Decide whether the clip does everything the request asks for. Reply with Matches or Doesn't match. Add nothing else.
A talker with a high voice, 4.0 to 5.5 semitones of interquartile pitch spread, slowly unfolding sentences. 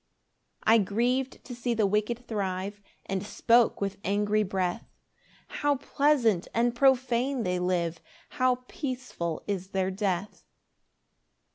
Matches